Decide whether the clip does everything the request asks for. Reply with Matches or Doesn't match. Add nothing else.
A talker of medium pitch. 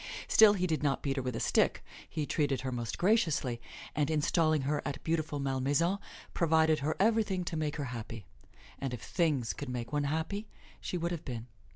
Matches